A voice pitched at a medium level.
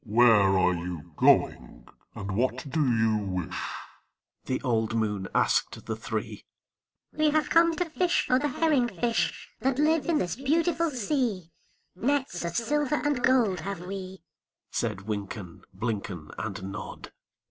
Yes: medium, 180 Hz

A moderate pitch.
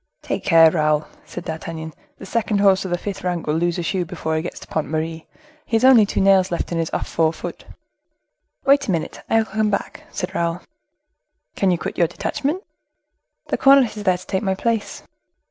Yes: medium, 180 Hz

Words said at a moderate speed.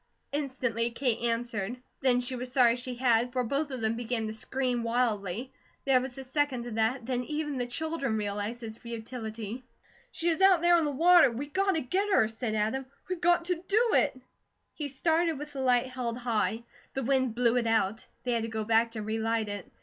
No: fast, 210 wpm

